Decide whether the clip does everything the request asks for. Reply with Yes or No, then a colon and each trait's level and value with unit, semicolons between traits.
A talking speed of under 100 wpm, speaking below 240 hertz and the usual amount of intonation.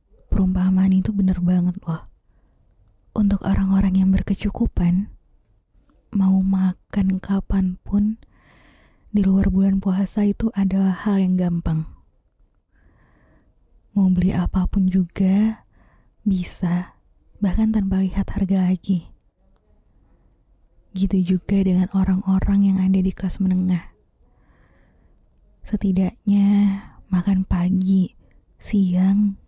No: average, 90 wpm; high, 190 Hz; narrow, 1.5 semitones